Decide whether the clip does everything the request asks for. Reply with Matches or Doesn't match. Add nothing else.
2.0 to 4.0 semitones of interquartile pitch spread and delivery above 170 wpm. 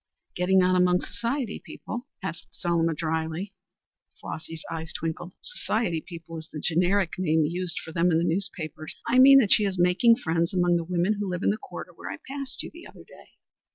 Matches